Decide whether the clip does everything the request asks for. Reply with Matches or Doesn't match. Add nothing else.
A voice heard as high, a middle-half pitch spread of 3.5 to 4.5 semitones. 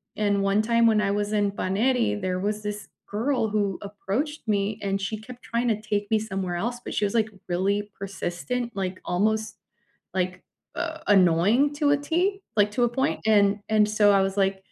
Doesn't match